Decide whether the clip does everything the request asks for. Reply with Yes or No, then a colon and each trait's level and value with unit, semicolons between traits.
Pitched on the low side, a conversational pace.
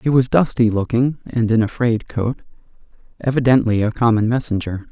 Yes: low, 115 Hz; average, 160 wpm